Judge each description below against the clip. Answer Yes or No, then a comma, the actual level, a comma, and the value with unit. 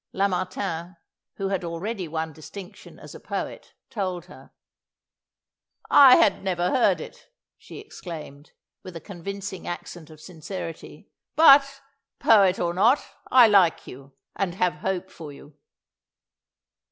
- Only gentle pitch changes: No, average, 3.2 semitones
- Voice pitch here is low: No, medium, 185 Hz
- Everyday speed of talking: No, slow, 130 wpm